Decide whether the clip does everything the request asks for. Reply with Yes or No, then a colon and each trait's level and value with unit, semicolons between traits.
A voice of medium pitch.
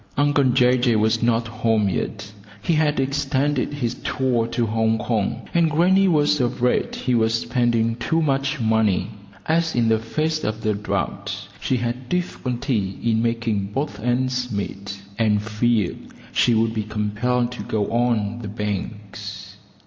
No: low, 120 Hz